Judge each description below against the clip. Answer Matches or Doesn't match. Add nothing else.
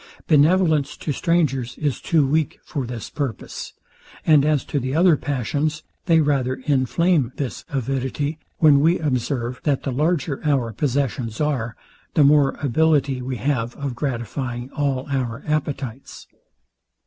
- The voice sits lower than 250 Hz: Matches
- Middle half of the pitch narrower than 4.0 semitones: Matches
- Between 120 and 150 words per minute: Matches